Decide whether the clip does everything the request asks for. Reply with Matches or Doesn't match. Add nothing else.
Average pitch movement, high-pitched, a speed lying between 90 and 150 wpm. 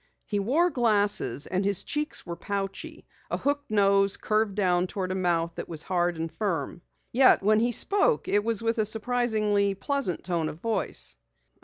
Doesn't match